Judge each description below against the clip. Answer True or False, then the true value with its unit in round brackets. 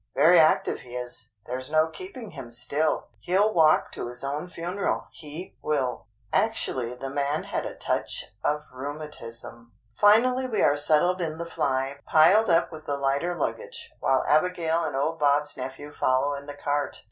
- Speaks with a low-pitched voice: False (150 Hz)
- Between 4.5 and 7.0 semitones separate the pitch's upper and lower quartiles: False (4.0 semitones)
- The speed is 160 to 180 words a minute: True (170 wpm)